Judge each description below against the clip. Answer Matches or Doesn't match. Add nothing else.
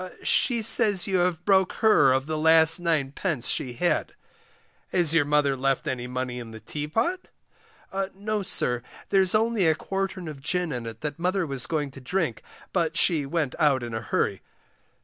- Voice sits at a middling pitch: Matches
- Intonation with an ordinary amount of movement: Doesn't match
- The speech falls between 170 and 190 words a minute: Matches